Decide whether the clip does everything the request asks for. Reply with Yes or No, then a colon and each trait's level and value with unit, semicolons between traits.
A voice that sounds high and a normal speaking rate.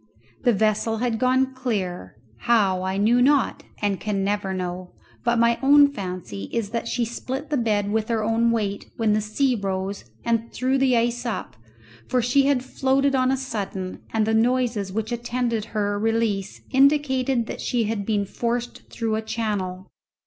Yes: high, 225 Hz; average, 175 wpm